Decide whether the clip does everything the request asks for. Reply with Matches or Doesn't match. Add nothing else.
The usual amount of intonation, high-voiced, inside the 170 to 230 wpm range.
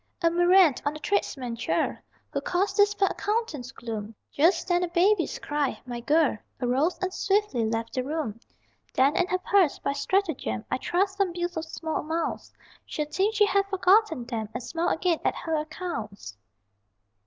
Doesn't match